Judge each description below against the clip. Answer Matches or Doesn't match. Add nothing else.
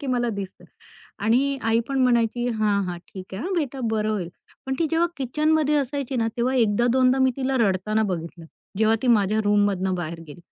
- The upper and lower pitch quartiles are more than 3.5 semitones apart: Matches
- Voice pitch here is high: Matches